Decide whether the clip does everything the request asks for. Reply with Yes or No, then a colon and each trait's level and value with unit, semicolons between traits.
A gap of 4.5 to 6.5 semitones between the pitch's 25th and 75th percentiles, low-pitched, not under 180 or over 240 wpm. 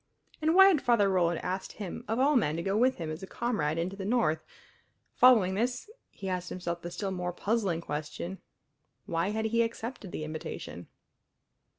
No: average, 5.3 semitones; high, 190 Hz; average, 185 wpm